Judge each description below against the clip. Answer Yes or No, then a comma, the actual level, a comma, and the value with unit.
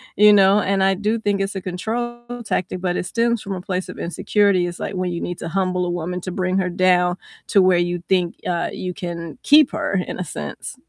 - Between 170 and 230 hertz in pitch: Yes, medium, 185 Hz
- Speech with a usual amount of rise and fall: No, narrow, 1.9 semitones